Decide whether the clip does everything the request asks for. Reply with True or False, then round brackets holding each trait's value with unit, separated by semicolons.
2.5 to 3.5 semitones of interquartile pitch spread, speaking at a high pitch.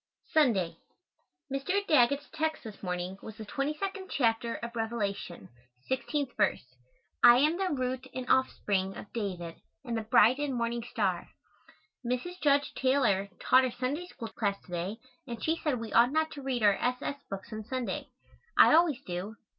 False (5.3 semitones; 240 Hz)